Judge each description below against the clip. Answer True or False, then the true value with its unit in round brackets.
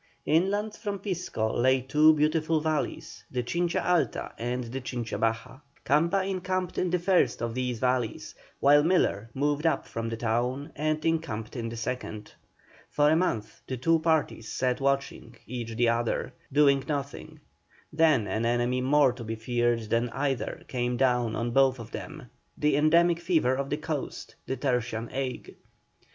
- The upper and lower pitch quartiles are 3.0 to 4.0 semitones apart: False (4.7 semitones)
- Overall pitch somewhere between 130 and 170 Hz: True (135 Hz)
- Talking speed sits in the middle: True (165 wpm)